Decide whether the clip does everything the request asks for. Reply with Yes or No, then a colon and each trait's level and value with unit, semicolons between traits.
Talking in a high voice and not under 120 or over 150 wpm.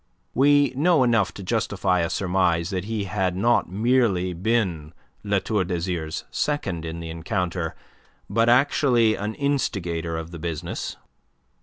No: very low, 95 Hz; average, 140 wpm